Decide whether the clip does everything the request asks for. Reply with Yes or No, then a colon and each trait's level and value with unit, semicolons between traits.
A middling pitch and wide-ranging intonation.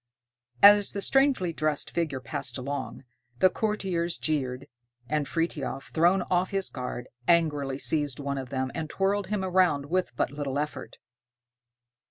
No: medium, 155 Hz; average, 5.0 semitones